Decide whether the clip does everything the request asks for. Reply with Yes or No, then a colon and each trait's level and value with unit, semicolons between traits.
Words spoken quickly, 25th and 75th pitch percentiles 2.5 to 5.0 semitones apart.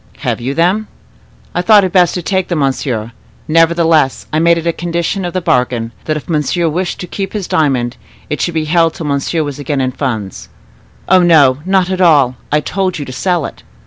Yes: fast, 210 wpm; average, 4.2 semitones